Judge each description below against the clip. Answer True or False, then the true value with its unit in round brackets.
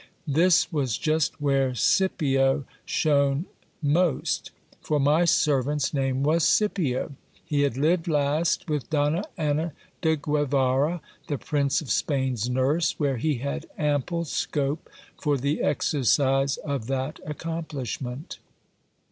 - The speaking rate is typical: False (120 wpm)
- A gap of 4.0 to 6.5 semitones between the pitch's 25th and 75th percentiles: False (2.6 semitones)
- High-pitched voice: False (145 Hz)